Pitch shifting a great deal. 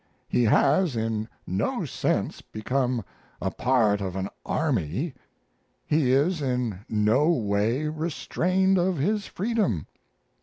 Yes: wide, 7.3 semitones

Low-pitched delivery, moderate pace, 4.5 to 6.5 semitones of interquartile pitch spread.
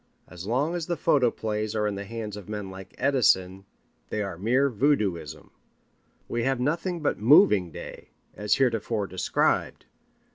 Yes: low, 110 Hz; average, 150 wpm; wide, 5.6 semitones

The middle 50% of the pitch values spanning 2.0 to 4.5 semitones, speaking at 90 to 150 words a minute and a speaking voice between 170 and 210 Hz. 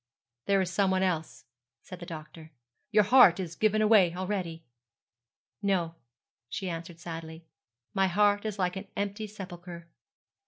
Yes: average, 3.1 semitones; average, 145 wpm; medium, 185 Hz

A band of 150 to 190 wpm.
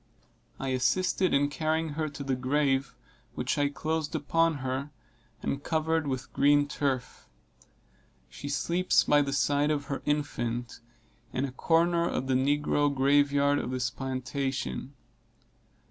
No: average, 140 wpm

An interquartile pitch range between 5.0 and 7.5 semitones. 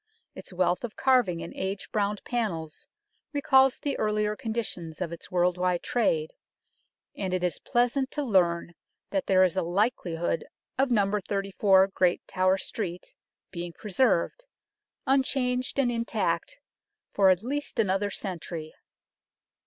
Yes: wide, 5.4 semitones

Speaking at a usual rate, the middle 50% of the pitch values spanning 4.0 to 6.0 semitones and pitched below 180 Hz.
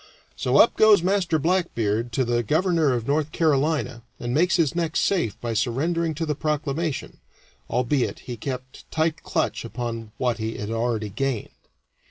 Yes: average, 160 wpm; wide, 5.5 semitones; medium, 140 Hz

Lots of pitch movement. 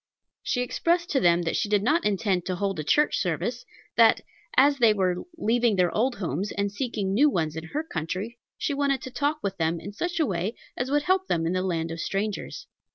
Yes: wide, 7.2 semitones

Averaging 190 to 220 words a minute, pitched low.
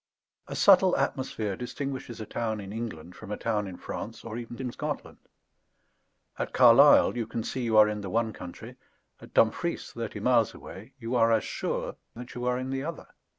Yes: average, 195 wpm; low, 115 Hz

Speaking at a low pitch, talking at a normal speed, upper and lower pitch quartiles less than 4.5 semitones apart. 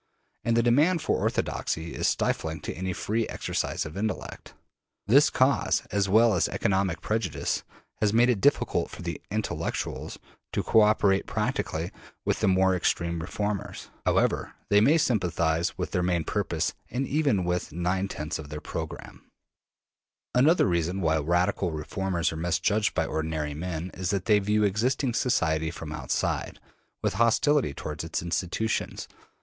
No: very low, 95 Hz; average, 155 wpm; average, 5.1 semitones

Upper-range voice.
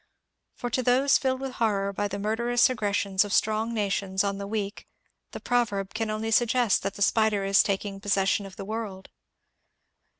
Yes: high, 210 Hz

